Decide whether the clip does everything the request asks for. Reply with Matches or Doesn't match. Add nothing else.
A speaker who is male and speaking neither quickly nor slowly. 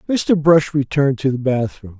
Matches